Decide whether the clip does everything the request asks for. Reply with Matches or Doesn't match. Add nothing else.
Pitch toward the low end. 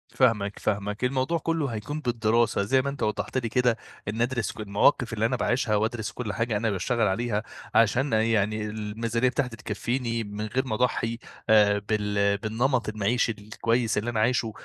Matches